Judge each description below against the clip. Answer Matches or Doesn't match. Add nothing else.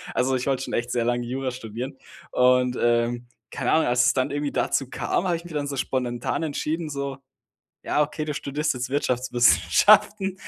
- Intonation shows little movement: Doesn't match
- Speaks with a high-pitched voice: Doesn't match